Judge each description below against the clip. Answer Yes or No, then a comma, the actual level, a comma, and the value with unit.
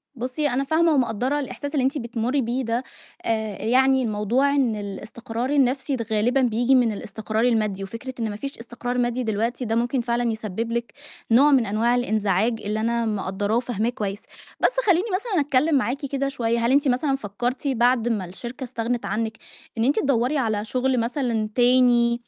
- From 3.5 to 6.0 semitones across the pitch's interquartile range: No, average, 2.9 semitones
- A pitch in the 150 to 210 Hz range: No, high, 240 Hz